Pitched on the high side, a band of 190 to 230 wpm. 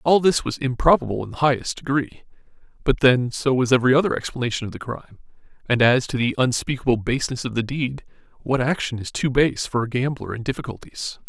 No: low, 130 Hz; average, 195 wpm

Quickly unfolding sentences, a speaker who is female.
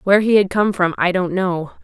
Yes: fast, 260 wpm; female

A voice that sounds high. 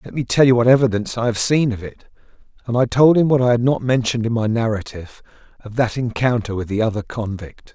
No: low, 115 Hz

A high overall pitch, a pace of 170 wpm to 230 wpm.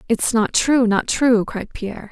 Yes: high, 230 Hz; average, 200 wpm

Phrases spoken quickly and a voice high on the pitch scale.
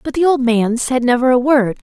Yes: fast, 250 wpm; very high, 255 Hz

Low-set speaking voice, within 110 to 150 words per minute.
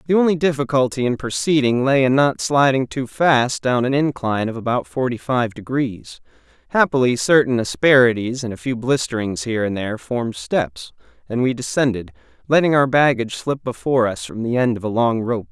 No: low, 125 Hz; average, 180 wpm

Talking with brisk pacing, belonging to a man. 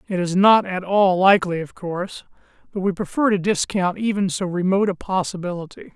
No: average, 180 wpm; male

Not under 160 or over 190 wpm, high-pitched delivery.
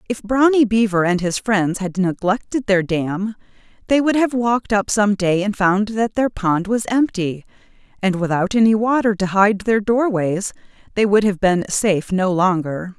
Yes: average, 180 wpm; high, 205 Hz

